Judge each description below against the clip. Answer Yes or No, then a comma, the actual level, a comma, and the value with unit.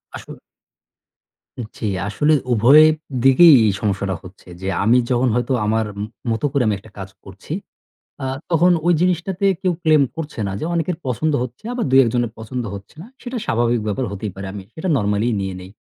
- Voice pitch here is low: Yes, low, 120 Hz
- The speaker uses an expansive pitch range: Yes, wide, 7.1 semitones